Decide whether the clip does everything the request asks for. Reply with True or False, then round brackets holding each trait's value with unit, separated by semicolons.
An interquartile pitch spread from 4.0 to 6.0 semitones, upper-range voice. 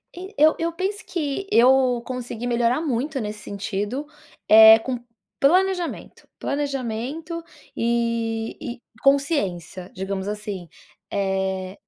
True (5.6 semitones; 240 Hz)